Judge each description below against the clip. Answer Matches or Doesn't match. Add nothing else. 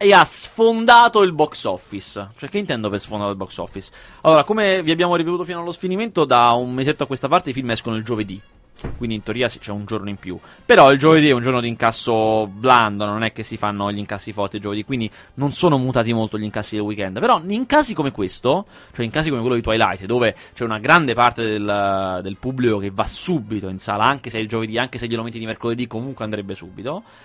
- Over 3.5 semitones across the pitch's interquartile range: Matches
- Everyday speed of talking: Doesn't match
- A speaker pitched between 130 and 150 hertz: Doesn't match